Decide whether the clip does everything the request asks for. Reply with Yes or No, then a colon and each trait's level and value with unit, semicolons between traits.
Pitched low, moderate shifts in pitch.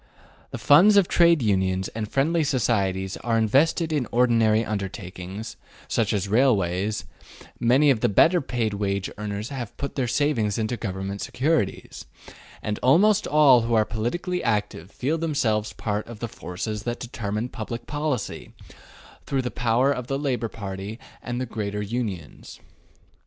Yes: low, 115 Hz; average, 4.7 semitones